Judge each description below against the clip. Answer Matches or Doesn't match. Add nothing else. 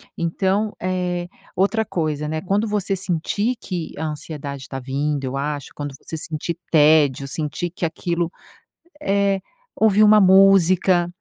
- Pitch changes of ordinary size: Matches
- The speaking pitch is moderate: Matches